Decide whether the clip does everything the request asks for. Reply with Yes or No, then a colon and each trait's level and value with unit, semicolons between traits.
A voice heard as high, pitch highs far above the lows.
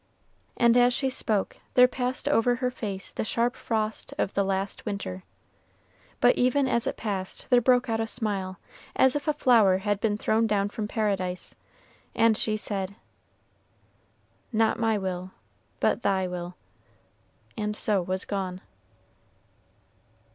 No: high, 215 Hz; average, 3.8 semitones